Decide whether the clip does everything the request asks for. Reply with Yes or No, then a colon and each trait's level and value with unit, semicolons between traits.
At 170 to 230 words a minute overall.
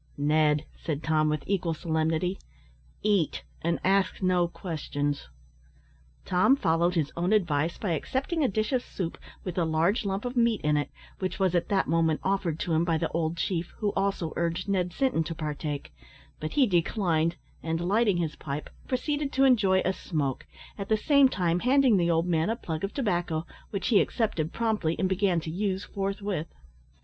Yes: average, 180 wpm